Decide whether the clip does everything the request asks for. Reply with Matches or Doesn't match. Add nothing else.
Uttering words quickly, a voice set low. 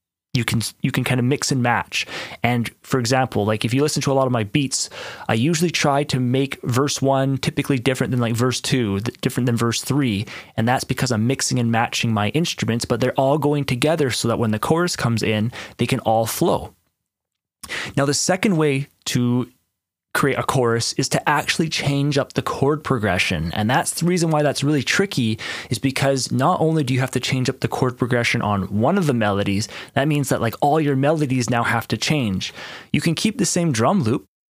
Matches